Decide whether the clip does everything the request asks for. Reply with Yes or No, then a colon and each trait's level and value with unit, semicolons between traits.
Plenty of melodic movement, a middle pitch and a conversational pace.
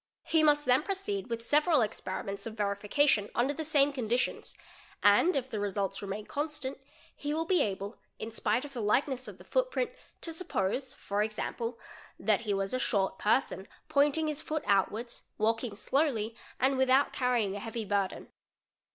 No: wide, 5.8 semitones; high, 245 Hz; average, 170 wpm